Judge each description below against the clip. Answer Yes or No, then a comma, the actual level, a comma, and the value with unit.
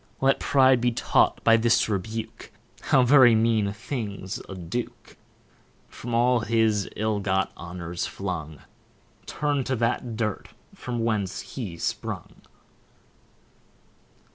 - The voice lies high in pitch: No, low, 110 Hz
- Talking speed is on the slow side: Yes, slow, 120 wpm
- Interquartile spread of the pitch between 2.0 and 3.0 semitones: No, average, 3.6 semitones